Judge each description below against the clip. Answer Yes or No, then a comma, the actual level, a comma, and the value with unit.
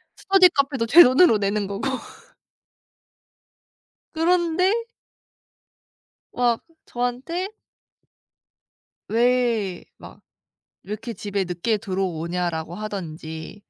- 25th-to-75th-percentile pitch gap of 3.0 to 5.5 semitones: No, wide, 5.9 semitones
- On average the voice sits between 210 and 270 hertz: Yes, high, 220 Hz